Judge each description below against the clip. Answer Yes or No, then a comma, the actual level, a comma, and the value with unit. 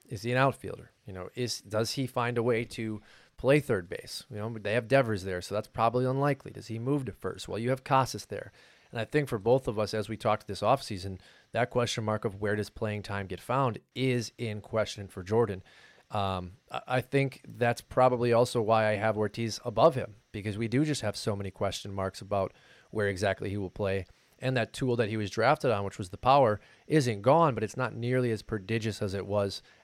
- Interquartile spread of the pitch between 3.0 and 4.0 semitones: Yes, average, 3.4 semitones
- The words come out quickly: Yes, fast, 225 wpm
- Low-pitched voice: Yes, low, 110 Hz